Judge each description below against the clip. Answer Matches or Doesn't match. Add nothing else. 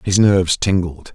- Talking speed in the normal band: Matches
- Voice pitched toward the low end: Matches